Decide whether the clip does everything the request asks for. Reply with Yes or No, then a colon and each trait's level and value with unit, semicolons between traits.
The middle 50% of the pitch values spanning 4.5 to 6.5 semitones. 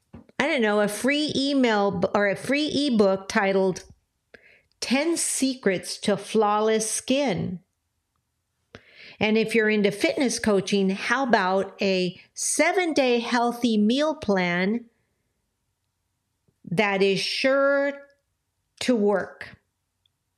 Yes: average, 4.8 semitones